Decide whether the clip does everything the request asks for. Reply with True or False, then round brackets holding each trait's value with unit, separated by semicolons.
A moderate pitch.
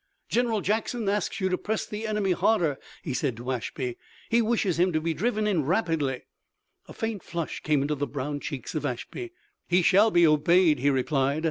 True (170 Hz)